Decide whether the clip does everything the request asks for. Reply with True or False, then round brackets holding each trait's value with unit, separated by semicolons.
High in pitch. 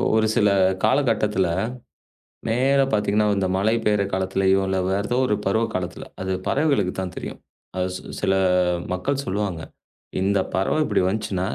False (100 Hz)